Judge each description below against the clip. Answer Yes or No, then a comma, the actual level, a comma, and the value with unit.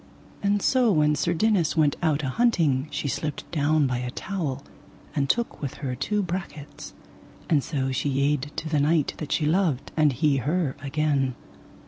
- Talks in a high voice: No, medium, 150 Hz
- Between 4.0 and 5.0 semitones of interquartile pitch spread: No, average, 3.4 semitones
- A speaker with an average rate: Yes, average, 175 wpm